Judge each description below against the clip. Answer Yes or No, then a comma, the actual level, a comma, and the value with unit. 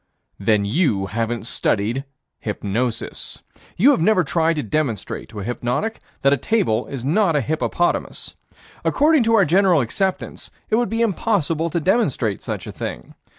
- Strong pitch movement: Yes, wide, 8.9 semitones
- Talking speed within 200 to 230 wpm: No, average, 155 wpm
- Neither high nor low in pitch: Yes, medium, 150 Hz